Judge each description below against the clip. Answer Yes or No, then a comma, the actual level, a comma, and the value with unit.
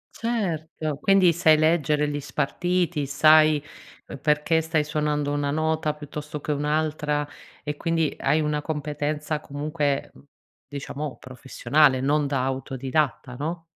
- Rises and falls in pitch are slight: Yes, narrow, 1.5 semitones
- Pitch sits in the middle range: Yes, medium, 150 Hz